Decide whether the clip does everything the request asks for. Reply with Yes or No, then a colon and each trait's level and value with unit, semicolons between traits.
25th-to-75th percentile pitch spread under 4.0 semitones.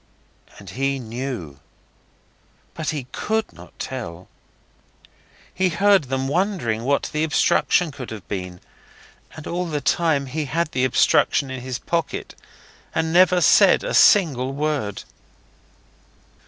No: average, 5.1 semitones